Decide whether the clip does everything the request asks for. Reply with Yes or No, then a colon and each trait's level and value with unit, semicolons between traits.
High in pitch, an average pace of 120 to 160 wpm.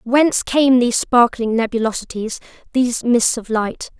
Yes: high, 240 Hz; slow, 135 wpm